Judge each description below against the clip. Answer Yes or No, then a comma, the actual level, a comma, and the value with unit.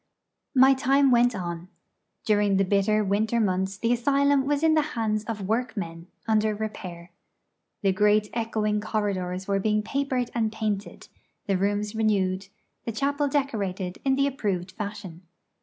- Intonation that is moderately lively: Yes, average, 3.8 semitones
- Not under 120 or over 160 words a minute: Yes, average, 145 wpm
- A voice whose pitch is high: Yes, high, 215 Hz